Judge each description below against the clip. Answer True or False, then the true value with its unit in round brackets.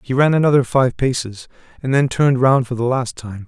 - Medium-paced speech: False (225 wpm)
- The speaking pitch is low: True (125 Hz)